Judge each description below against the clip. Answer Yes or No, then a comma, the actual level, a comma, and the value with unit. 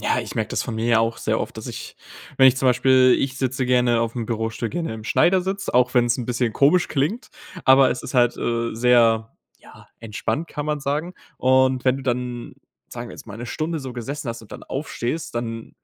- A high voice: No, low, 125 Hz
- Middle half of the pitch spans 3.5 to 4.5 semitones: No, average, 2.7 semitones